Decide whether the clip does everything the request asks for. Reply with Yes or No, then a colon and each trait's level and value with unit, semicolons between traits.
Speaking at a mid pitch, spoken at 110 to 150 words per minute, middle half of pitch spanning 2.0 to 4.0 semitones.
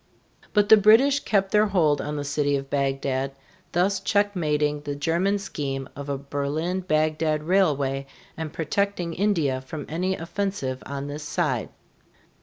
No: medium, 155 Hz; average, 145 wpm; average, 5.1 semitones